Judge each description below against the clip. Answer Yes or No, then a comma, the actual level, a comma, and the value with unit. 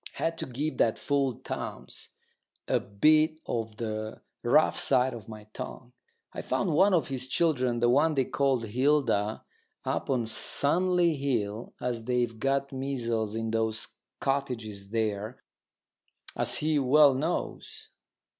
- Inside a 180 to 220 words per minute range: No, slow, 135 wpm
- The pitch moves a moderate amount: Yes, average, 4.1 semitones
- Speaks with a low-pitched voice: Yes, low, 125 Hz